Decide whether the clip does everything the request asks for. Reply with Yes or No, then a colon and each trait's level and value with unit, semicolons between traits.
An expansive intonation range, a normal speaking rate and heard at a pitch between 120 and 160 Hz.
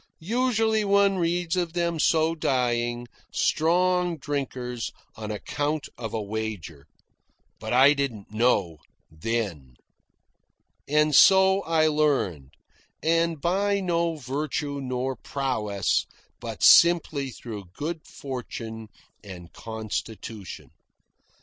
No: wide, 7.1 semitones; slow, 100 wpm; medium, 140 Hz